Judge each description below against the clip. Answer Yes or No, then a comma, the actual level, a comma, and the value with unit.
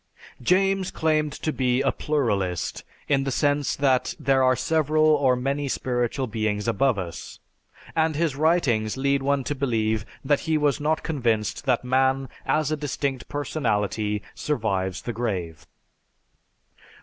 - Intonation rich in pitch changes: No, average, 4.6 semitones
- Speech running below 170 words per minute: Yes, average, 140 wpm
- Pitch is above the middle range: No, low, 135 Hz